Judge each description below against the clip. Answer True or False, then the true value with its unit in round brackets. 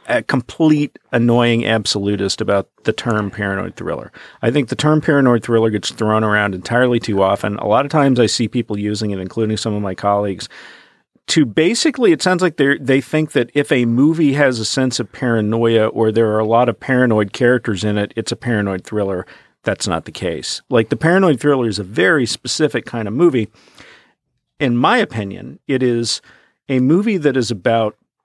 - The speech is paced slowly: False (195 wpm)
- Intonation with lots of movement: False (3.9 semitones)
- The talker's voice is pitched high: False (115 Hz)